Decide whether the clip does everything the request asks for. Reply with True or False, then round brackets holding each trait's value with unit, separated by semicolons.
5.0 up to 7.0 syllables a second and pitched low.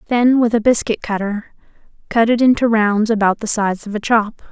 False (5.1 syllables/s; 220 Hz)